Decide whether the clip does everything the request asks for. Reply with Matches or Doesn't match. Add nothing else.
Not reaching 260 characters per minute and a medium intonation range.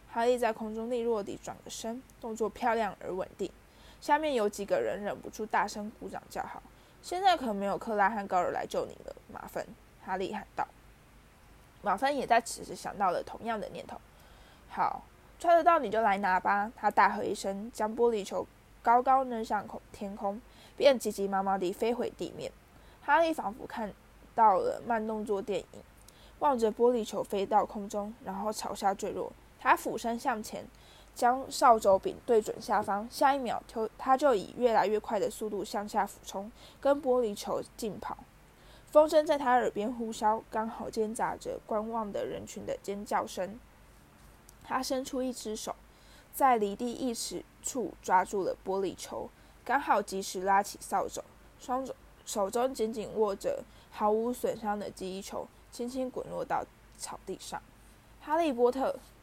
Matches